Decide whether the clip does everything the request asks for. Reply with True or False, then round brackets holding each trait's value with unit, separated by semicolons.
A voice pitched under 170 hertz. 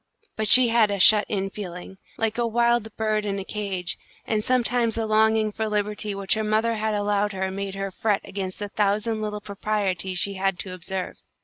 False (210 Hz)